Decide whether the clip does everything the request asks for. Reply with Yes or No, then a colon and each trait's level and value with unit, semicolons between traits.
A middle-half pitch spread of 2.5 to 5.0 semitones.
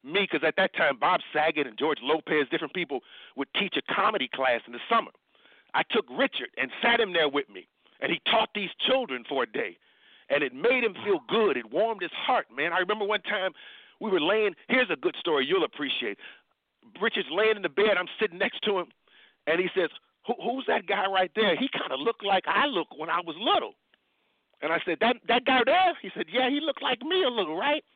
No: wide, 5.6 semitones